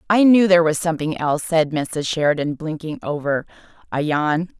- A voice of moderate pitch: Yes, medium, 160 Hz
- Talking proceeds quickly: No, average, 170 wpm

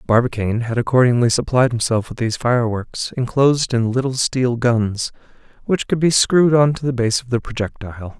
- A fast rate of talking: No, average, 175 wpm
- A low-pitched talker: Yes, low, 120 Hz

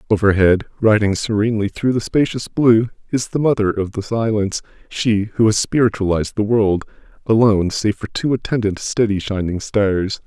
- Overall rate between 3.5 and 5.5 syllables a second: Yes, 5.2 syllables/s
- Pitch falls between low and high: No, low, 110 Hz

